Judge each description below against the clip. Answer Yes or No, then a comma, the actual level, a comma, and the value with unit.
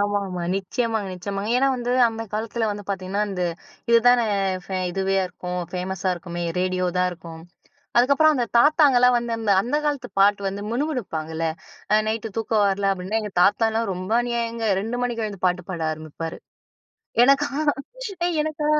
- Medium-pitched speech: No, high, 210 Hz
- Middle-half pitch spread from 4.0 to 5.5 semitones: Yes, average, 4.4 semitones